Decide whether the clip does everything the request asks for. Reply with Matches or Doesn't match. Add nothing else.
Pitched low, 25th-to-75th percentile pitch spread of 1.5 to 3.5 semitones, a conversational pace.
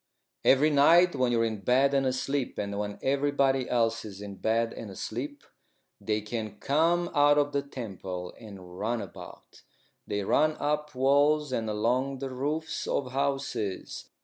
Doesn't match